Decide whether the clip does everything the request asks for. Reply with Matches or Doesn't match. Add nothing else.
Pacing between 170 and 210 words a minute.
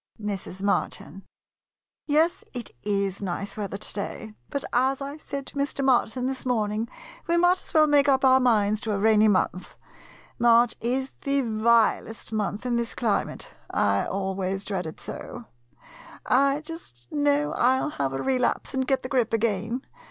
Matches